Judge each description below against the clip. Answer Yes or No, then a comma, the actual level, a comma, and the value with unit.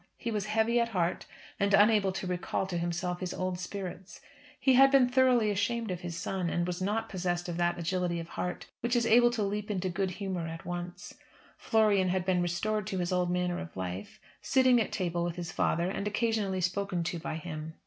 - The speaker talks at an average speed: No, fast, 210 wpm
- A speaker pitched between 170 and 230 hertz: Yes, medium, 185 Hz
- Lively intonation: No, average, 3.3 semitones